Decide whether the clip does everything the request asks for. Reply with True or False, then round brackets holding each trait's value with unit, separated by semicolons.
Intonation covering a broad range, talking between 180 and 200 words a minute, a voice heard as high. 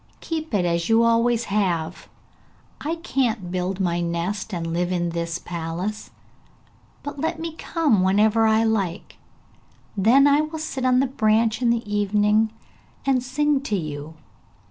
False (6.2 semitones; 155 wpm; 215 Hz)